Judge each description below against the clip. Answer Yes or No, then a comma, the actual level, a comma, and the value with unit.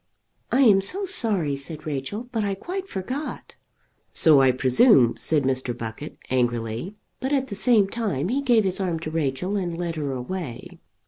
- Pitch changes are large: Yes, wide, 8.6 semitones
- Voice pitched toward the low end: No, medium, 175 Hz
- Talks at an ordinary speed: Yes, average, 175 wpm